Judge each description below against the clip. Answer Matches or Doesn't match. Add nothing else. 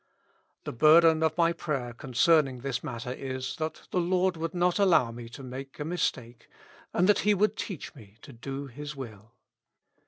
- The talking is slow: Doesn't match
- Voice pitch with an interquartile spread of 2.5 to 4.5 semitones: Doesn't match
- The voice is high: Doesn't match